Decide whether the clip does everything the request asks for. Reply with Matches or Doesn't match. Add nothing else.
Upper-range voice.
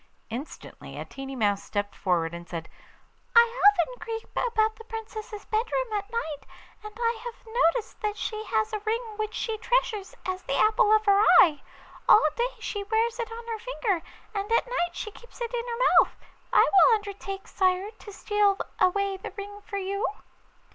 Matches